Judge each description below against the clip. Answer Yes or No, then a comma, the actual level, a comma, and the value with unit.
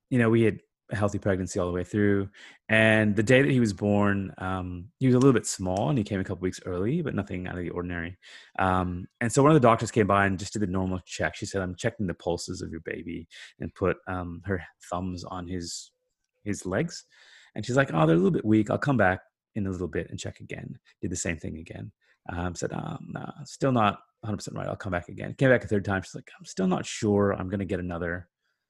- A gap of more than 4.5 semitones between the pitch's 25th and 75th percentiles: No, average, 3.6 semitones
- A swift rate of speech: Yes, fast, 255 wpm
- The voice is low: Yes, low, 100 Hz